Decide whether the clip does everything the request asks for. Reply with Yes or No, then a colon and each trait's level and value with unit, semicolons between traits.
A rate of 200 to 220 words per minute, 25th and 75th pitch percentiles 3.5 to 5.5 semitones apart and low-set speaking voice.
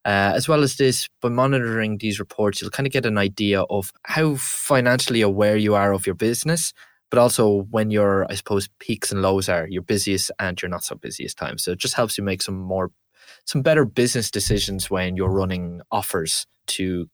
Yes: fast, 205 wpm; average, 4.2 semitones; low, 105 Hz